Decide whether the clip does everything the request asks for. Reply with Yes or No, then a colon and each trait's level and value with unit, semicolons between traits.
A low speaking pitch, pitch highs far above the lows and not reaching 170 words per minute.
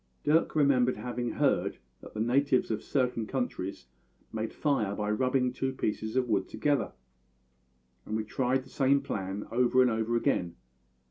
No: low, 125 Hz; average, 3.5 semitones; average, 155 wpm